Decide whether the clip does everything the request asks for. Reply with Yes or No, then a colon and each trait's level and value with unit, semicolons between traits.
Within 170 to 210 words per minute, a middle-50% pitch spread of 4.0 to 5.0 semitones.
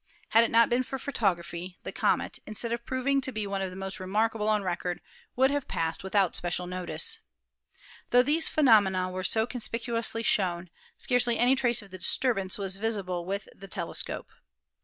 Yes: average, 180 wpm; average, 4.4 semitones